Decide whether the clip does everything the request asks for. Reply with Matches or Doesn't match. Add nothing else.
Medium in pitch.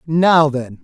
Matches